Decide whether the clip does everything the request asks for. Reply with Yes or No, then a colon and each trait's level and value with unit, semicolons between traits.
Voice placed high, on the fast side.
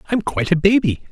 No: medium, 180 Hz; fast, 215 wpm